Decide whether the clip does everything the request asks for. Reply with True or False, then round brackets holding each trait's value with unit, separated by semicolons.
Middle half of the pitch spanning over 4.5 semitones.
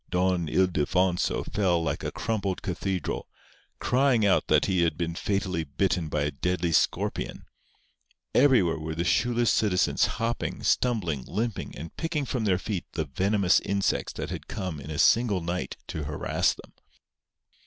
False (4.2 semitones)